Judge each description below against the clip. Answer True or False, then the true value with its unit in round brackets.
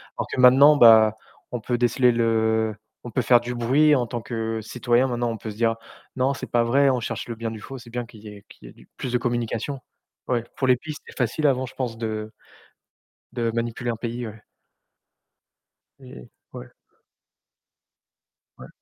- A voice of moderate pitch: False (120 Hz)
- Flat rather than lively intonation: True (2.1 semitones)